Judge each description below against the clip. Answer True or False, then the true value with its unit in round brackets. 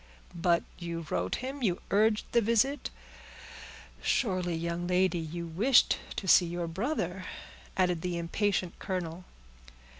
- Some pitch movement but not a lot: True (3.4 semitones)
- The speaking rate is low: True (120 wpm)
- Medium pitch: True (180 Hz)